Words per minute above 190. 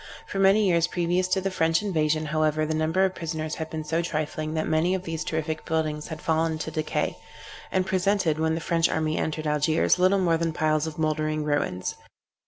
Yes: average, 200 wpm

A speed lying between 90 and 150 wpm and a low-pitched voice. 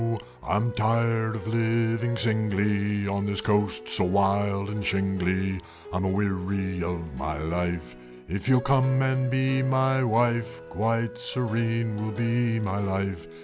Yes: average, 145 wpm; low, 105 Hz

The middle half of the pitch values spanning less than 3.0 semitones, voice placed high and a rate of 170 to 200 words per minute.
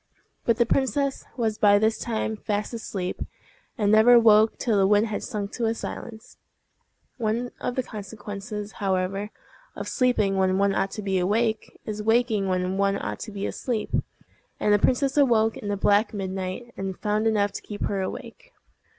Yes: narrow, 2.4 semitones; high, 210 Hz; average, 175 wpm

